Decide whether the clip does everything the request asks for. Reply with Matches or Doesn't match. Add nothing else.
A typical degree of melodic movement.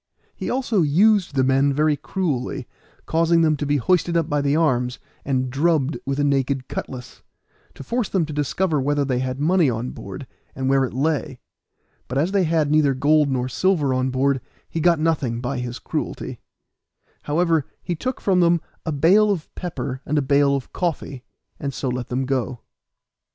Matches